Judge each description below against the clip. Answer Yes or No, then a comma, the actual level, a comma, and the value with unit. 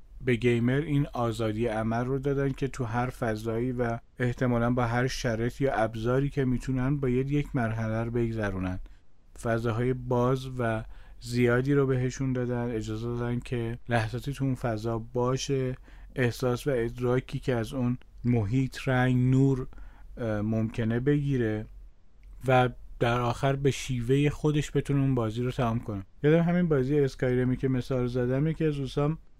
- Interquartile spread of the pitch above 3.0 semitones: No, narrow, 2.4 semitones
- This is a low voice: Yes, low, 125 Hz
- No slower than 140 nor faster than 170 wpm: Yes, average, 150 wpm